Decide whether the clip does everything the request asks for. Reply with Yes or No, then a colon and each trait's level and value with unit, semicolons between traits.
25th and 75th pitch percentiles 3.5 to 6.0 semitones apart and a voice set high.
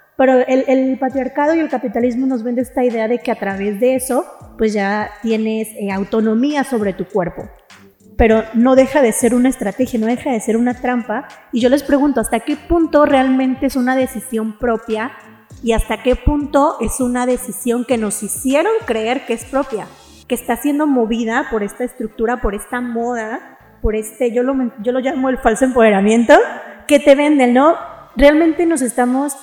No: average, 3.0 semitones; high, 245 Hz